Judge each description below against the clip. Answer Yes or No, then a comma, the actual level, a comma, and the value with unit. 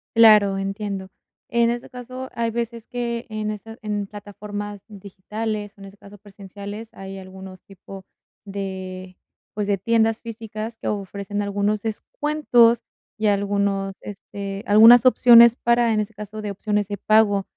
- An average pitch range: No, narrow, 2.3 semitones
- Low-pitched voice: No, high, 205 Hz